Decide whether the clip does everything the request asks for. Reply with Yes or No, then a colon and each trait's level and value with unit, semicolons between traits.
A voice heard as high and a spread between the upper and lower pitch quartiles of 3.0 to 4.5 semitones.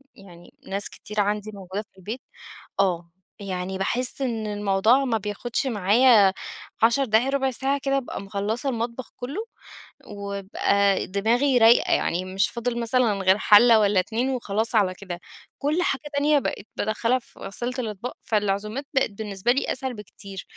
Yes: high, 215 Hz; average, 3.9 semitones